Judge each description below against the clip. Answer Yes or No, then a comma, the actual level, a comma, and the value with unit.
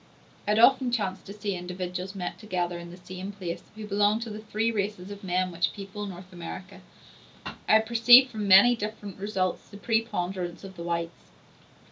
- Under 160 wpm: No, average, 185 wpm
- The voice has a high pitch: Yes, high, 195 Hz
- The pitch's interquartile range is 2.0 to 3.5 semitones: Yes, average, 2.9 semitones